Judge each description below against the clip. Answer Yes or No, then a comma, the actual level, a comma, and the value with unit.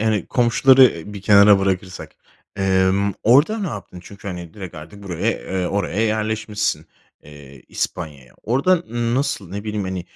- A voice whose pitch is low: Yes, low, 100 Hz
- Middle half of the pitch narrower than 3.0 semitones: No, average, 3.3 semitones